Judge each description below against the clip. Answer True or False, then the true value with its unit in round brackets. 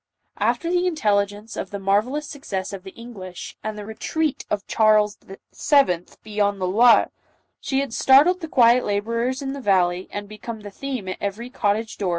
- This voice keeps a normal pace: True (170 wpm)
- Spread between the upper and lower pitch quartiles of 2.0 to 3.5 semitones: False (4.5 semitones)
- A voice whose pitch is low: False (215 Hz)